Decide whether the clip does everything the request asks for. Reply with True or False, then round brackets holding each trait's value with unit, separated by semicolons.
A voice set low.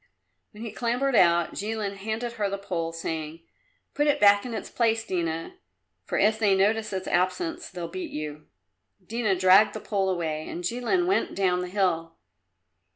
False (195 Hz)